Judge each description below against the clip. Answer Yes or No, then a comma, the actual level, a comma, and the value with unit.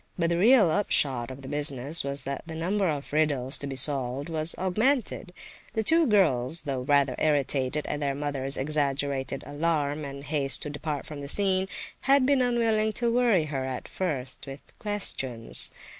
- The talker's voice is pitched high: No, medium, 150 Hz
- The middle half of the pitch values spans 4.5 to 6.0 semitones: Yes, wide, 5.5 semitones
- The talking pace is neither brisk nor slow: Yes, average, 175 wpm